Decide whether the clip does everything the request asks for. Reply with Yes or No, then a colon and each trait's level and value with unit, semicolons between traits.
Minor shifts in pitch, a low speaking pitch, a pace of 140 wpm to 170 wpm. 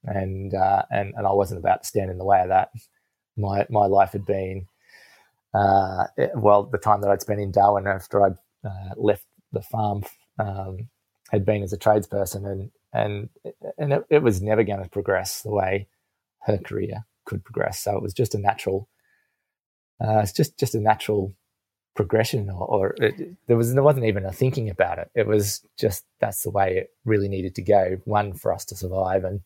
No: narrow, 1.8 semitones; low, 100 Hz; fast, 205 wpm